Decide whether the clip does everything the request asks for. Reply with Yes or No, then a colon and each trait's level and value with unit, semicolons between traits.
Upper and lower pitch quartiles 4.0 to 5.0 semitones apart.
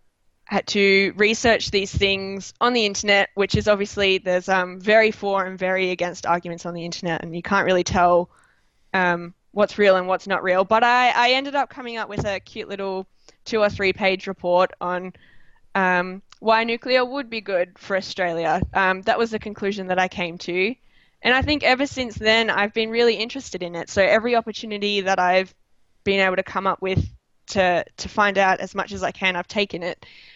No: average, 2.7 semitones